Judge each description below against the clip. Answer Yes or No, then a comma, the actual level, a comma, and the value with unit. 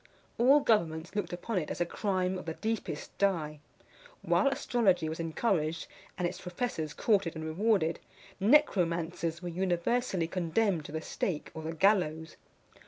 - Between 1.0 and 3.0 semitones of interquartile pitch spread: No, average, 4.2 semitones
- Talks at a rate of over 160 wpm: No, average, 150 wpm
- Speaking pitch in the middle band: Yes, medium, 175 Hz